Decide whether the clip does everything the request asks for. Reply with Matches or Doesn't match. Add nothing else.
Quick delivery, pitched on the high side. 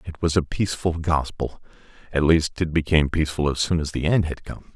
Doesn't match